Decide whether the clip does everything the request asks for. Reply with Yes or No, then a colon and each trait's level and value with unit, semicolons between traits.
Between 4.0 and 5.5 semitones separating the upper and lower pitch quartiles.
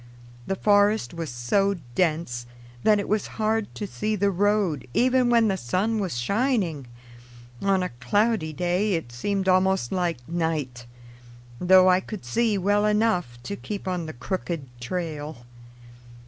Yes: average, 4.7 semitones